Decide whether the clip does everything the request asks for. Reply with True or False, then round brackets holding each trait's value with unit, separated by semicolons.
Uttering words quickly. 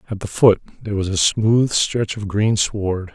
True (210 wpm)